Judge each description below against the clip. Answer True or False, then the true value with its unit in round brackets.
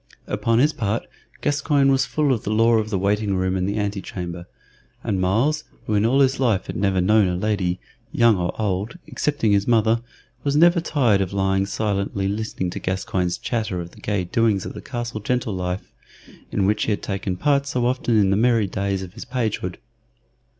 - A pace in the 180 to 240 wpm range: True (200 wpm)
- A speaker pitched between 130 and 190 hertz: False (105 Hz)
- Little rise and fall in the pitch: False (3.8 semitones)